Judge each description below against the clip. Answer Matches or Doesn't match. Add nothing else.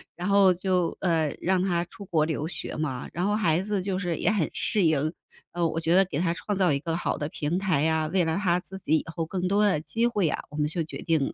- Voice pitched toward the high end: Doesn't match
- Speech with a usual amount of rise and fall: Matches